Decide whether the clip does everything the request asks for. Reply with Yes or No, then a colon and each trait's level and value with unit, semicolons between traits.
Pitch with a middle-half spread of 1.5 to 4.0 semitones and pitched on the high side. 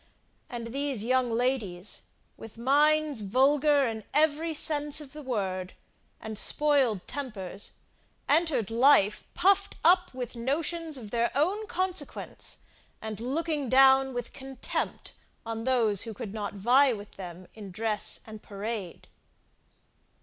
No: average, 5.1 semitones; very high, 255 Hz